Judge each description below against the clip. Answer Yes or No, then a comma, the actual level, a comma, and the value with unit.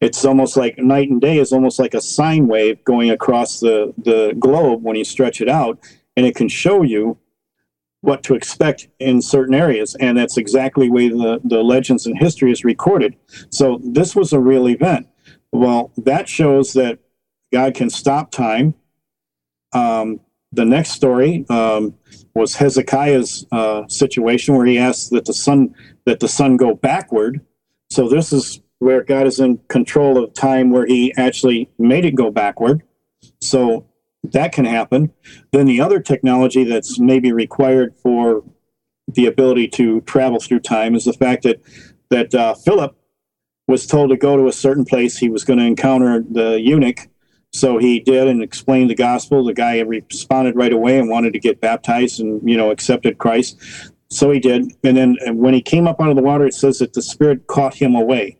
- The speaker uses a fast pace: No, average, 185 wpm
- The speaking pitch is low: Yes, low, 125 Hz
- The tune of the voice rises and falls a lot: No, narrow, 2.4 semitones